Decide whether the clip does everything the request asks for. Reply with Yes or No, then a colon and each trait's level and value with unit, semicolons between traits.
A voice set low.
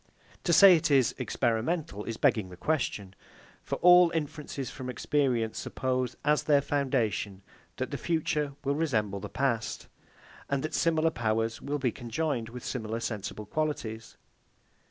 Yes: low, 130 Hz